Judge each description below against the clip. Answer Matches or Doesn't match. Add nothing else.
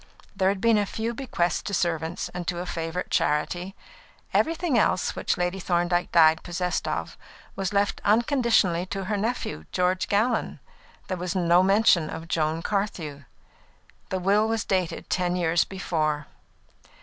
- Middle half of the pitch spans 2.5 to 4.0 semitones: Matches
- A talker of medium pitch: Matches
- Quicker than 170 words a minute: Doesn't match